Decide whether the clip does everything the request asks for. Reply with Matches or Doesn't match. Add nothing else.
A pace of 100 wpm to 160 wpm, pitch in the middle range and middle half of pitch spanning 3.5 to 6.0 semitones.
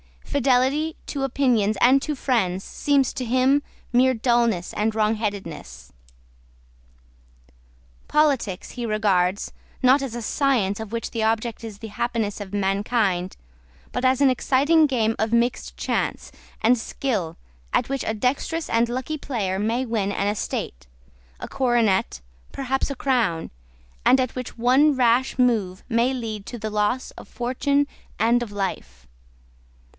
Doesn't match